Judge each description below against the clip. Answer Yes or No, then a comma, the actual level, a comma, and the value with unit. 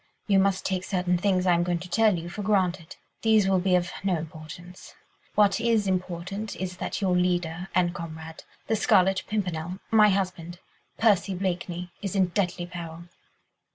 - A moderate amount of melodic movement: No, narrow, 2.1 semitones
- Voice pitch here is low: No, medium, 180 Hz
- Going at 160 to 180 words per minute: Yes, average, 170 wpm